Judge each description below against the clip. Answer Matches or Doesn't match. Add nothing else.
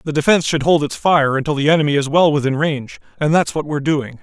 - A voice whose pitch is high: Doesn't match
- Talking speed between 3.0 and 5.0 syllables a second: Doesn't match